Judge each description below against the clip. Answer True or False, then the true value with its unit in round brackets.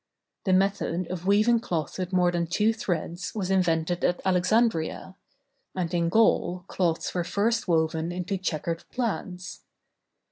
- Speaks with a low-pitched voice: False (180 Hz)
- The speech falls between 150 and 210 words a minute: False (140 wpm)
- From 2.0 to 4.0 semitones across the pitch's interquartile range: True (2.8 semitones)